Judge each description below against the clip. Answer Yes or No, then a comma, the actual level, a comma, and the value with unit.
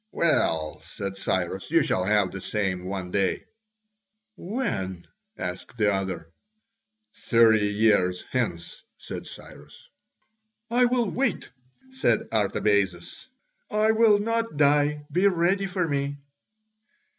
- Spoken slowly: Yes, slow, 110 wpm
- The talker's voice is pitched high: No, low, 110 Hz